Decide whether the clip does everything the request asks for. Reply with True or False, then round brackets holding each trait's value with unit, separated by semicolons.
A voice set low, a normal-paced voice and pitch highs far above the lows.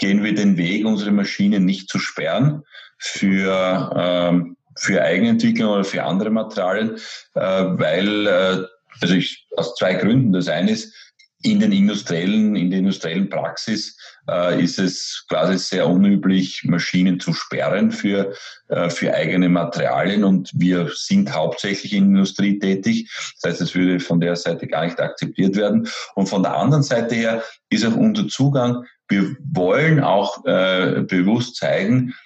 True (100 Hz; 150 wpm; 8.4 semitones)